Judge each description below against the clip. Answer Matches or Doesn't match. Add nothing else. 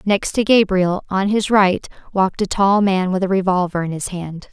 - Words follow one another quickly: Matches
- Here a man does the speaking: Doesn't match